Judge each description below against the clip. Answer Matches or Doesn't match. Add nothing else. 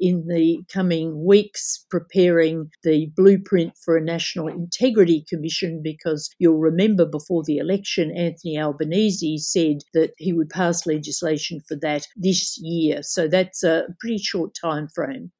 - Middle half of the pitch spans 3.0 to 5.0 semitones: Doesn't match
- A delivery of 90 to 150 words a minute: Matches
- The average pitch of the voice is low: Doesn't match